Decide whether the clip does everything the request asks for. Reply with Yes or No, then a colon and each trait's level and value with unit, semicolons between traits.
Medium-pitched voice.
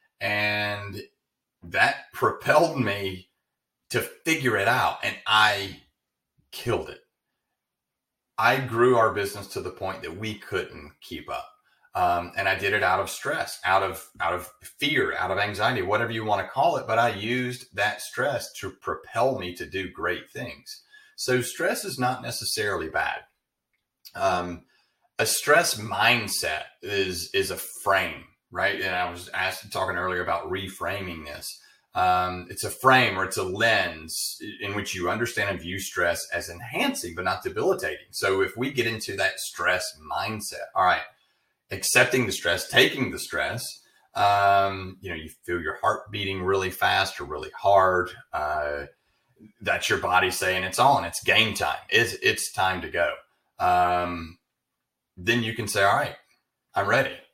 No: low, 100 Hz